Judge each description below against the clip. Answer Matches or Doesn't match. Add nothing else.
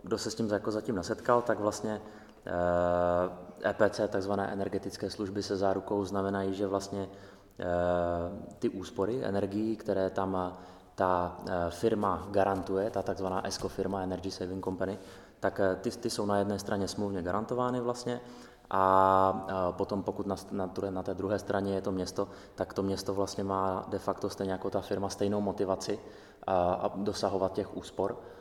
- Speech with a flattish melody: Matches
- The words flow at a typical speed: Matches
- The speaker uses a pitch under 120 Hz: Matches